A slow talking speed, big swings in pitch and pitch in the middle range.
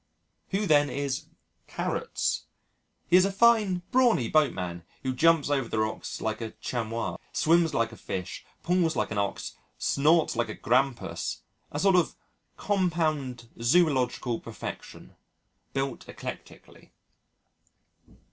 Yes: slow, 130 wpm; wide, 6.7 semitones; medium, 145 Hz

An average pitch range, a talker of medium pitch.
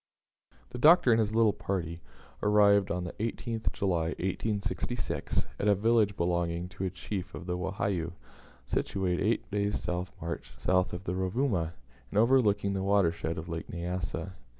No: average, 3.0 semitones; very low, 95 Hz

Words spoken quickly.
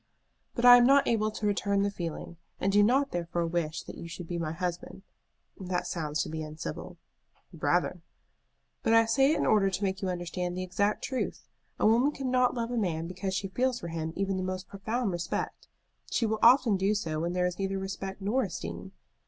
Yes: fast, 210 wpm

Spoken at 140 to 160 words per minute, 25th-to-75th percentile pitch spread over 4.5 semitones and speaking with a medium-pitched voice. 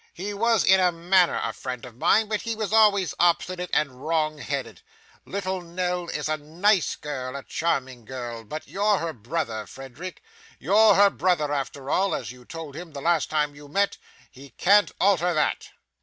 No: average, 185 wpm; average, 5.3 semitones; medium, 165 Hz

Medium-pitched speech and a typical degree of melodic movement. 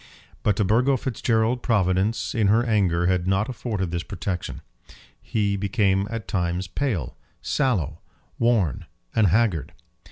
No: low, 100 Hz; average, 3.9 semitones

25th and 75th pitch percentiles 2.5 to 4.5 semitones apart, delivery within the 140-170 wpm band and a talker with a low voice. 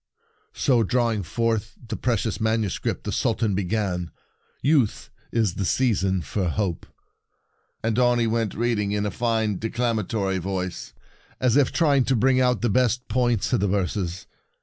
Yes: average, 3.7 semitones; average, 160 wpm; low, 110 Hz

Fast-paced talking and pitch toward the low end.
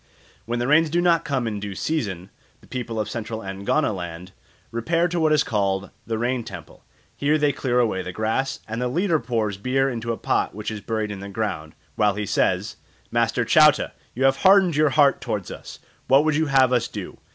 Yes: fast, 210 wpm; low, 120 Hz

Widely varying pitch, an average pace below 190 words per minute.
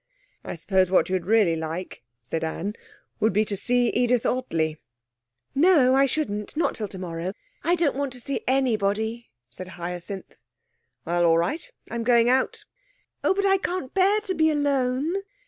Yes: wide, 7.2 semitones; average, 165 wpm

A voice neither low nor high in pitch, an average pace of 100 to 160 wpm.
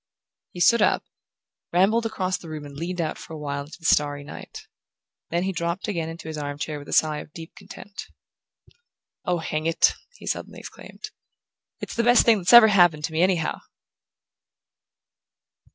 No: medium, 170 Hz; average, 175 wpm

